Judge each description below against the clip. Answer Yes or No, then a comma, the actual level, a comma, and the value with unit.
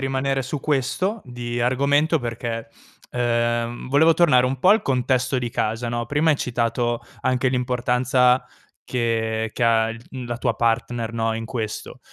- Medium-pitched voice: No, low, 125 Hz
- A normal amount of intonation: No, narrow, 2.2 semitones